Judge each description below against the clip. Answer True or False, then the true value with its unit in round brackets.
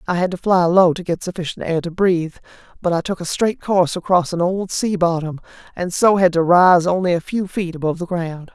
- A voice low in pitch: False (175 Hz)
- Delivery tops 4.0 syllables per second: True (5.7 syllables/s)